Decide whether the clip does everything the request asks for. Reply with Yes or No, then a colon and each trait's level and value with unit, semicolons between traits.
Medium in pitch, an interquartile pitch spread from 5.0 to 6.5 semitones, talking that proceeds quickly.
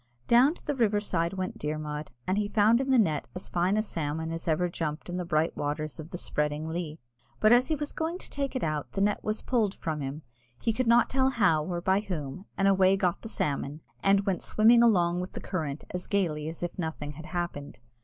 Yes: medium, 180 Hz; wide, 5.5 semitones; fast, 235 wpm